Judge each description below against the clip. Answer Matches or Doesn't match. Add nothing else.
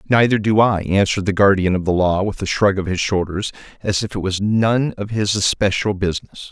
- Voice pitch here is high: Doesn't match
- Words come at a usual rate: Doesn't match